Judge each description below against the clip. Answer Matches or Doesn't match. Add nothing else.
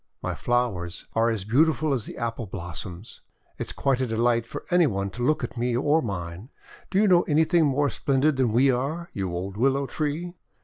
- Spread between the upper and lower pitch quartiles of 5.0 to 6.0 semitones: Matches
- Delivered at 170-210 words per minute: Matches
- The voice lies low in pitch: Matches